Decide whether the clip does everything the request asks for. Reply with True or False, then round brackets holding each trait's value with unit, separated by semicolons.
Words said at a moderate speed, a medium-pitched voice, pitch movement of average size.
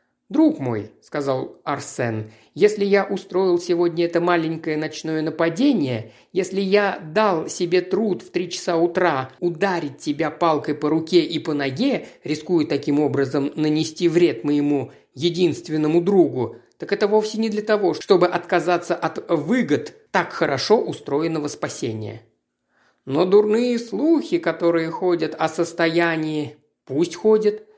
True (130 wpm; 170 Hz; 4.3 semitones)